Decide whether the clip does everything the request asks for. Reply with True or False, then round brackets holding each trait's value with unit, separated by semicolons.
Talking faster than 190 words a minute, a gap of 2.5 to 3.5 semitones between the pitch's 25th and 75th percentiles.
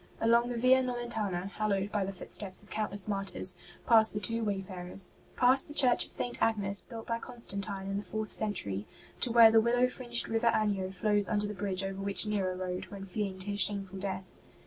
True (200 wpm; 2.8 semitones)